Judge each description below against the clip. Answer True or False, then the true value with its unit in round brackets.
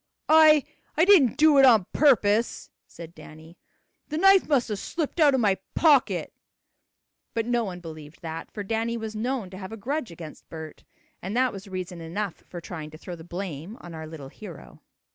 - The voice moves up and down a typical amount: False (7.4 semitones)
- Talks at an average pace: True (190 wpm)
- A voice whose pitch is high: True (205 Hz)